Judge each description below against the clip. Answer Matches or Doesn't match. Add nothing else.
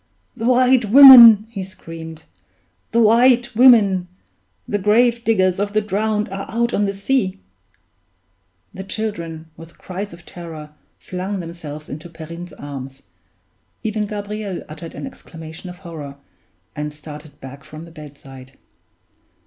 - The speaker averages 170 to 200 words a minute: Doesn't match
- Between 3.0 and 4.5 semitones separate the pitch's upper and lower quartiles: Doesn't match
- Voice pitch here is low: Doesn't match